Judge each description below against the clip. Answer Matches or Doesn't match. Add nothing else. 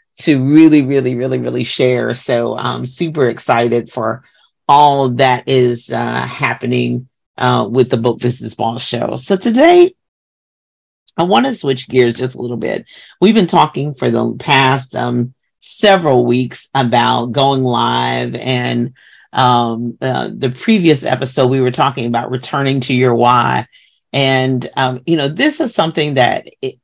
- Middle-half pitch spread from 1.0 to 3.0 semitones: Matches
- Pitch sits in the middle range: Doesn't match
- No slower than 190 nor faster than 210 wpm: Doesn't match